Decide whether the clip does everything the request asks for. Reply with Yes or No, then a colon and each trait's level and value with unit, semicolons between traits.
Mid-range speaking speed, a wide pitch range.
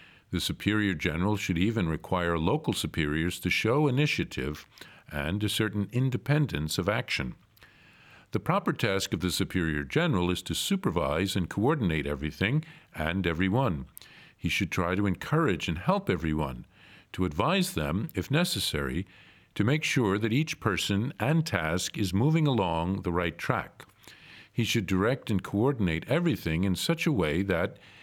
Yes: average, 150 wpm; wide, 6.7 semitones